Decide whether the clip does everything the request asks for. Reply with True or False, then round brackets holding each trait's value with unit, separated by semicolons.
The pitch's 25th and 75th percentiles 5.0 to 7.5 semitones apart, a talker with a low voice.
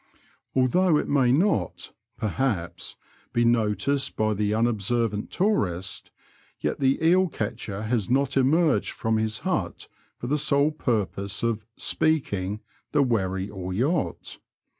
True (5.3 semitones; 115 Hz)